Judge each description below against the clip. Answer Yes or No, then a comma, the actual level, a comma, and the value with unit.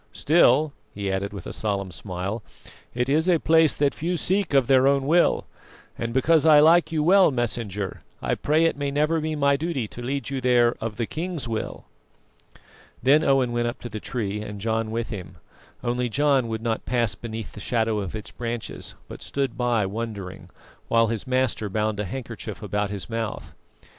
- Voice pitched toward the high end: No, low, 120 Hz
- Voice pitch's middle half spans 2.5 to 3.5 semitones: No, average, 4.7 semitones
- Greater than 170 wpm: Yes, average, 190 wpm